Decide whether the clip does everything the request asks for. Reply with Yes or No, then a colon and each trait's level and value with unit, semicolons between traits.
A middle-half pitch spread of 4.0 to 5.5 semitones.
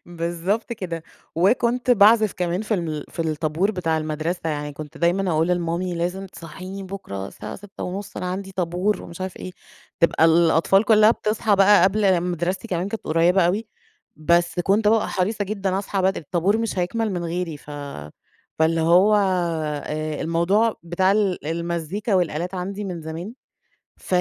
No: average, 3.1 semitones